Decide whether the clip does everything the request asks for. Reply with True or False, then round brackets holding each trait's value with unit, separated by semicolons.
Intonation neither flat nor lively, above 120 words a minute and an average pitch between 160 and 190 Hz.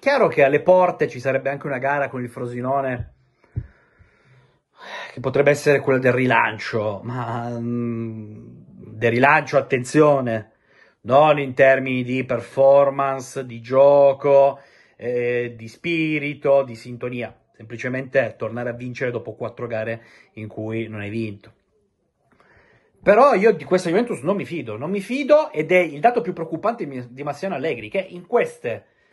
False (3.6 semitones; 145 wpm; 135 Hz)